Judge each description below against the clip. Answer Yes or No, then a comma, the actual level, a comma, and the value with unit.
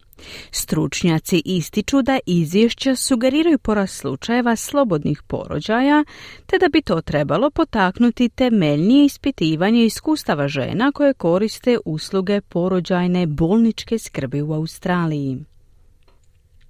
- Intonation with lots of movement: Yes, wide, 8.2 semitones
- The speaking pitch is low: No, high, 190 Hz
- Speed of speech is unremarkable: No, slow, 95 wpm